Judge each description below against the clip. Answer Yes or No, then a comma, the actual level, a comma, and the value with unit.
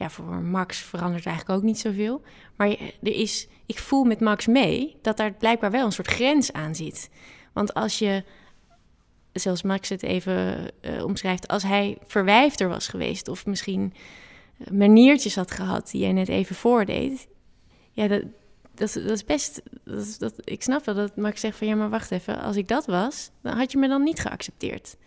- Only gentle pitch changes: No, average, 3.1 semitones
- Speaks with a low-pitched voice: No, high, 205 Hz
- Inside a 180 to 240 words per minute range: Yes, average, 190 wpm